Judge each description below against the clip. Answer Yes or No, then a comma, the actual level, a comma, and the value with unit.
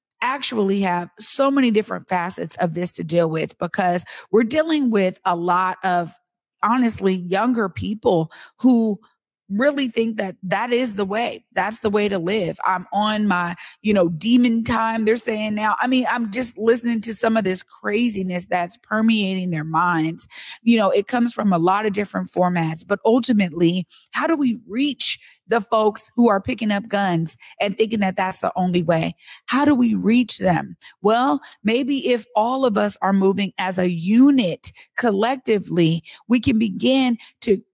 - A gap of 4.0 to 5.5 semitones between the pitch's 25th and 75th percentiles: Yes, average, 4.3 semitones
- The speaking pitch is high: Yes, high, 215 Hz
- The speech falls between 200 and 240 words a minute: No, average, 175 wpm